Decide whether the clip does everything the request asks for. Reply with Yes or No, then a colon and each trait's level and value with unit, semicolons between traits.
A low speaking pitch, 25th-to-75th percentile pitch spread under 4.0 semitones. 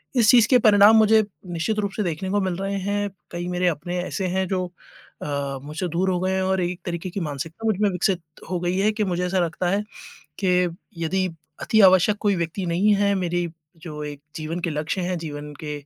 No: medium, 185 Hz; average, 2.8 semitones